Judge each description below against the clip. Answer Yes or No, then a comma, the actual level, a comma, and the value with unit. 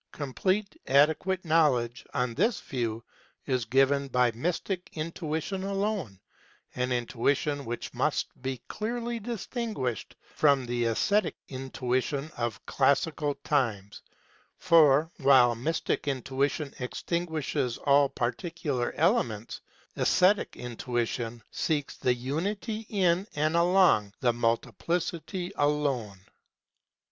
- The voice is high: No, medium, 140 Hz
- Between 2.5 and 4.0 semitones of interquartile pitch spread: No, wide, 5.6 semitones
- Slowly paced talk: Yes, slow, 100 wpm